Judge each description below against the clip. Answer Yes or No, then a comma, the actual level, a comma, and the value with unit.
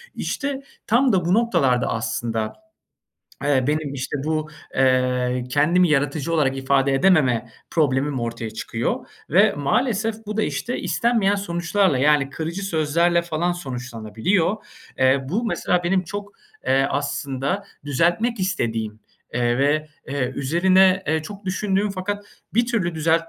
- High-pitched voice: No, medium, 155 Hz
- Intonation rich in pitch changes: Yes, wide, 6.3 semitones